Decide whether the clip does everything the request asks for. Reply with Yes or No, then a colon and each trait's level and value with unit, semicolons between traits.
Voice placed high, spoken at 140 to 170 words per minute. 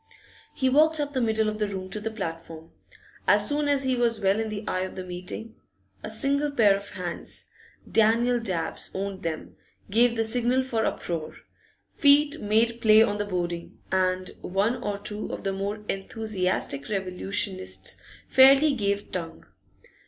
Yes: high, 210 Hz; average, 165 wpm